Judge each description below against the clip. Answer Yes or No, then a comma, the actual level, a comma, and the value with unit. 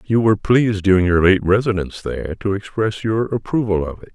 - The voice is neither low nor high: No, low, 100 Hz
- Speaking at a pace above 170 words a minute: Yes, fast, 205 wpm